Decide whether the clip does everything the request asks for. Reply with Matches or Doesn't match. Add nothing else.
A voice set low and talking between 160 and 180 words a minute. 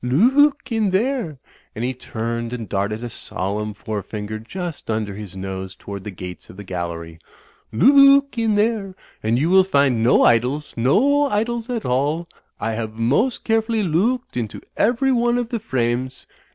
Matches